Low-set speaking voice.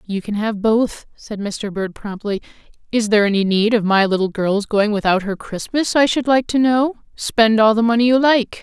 No: high, 220 Hz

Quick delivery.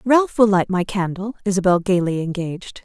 No: average, 170 wpm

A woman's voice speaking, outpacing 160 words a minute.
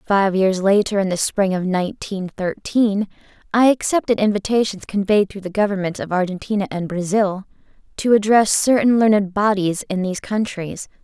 No: female; average, 150 wpm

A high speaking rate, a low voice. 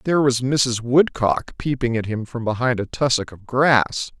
No: average, 185 wpm; low, 125 Hz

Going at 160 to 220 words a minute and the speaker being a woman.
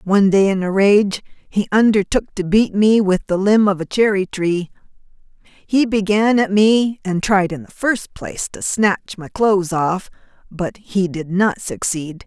Yes: average, 180 wpm; female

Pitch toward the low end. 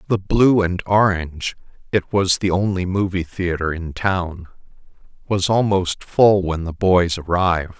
Yes: very low, 90 Hz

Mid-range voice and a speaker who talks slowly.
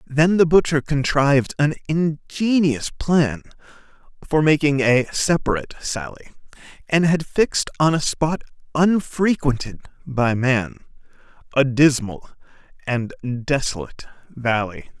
Yes: medium, 145 Hz; slow, 105 wpm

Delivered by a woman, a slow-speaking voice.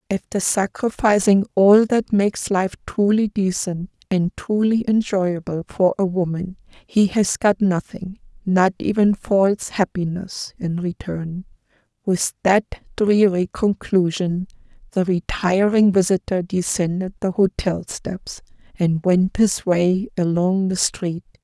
Yes: female; slow, 120 wpm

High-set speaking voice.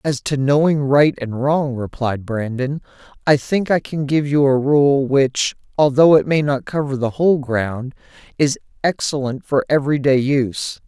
No: medium, 140 Hz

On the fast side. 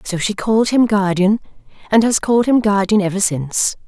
No: average, 185 wpm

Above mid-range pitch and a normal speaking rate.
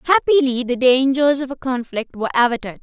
Yes: very high, 260 Hz; average, 170 wpm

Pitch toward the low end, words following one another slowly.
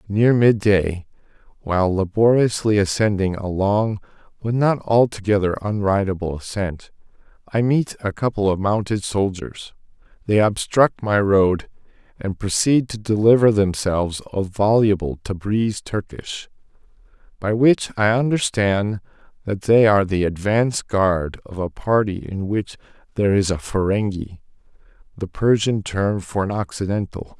Yes: low, 100 Hz; slow, 125 wpm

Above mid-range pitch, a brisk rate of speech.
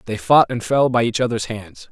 No: low, 115 Hz; fast, 250 wpm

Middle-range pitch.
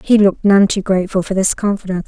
No: high, 195 Hz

